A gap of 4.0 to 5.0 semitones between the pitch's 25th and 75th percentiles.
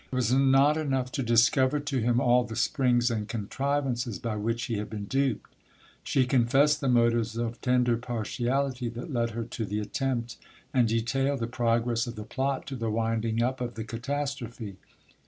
No: narrow, 2.5 semitones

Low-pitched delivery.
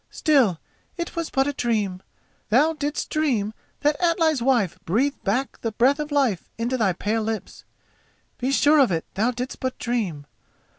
No: very high, 250 Hz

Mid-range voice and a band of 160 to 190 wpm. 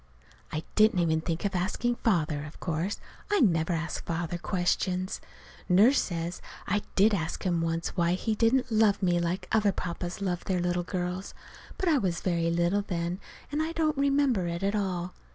Yes: medium, 180 Hz; average, 180 wpm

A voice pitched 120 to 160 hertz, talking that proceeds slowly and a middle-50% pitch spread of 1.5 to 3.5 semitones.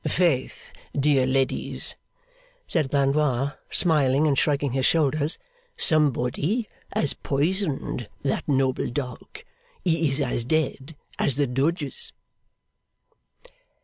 Yes: medium, 140 Hz; slow, 100 wpm; average, 2.7 semitones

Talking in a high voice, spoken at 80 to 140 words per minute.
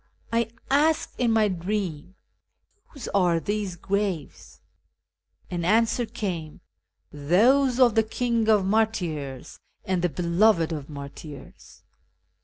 Yes: high, 195 Hz; slow, 135 wpm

